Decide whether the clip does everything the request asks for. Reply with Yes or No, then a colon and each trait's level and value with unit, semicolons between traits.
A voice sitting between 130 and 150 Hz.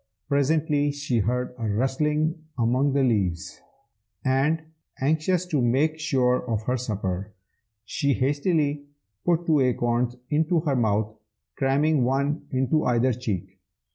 Yes: low, 135 Hz